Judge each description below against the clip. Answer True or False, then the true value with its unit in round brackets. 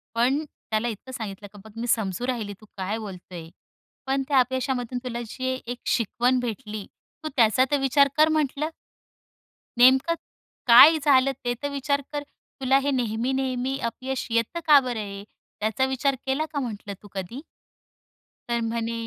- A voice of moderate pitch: False (250 Hz)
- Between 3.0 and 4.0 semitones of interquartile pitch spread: True (3.4 semitones)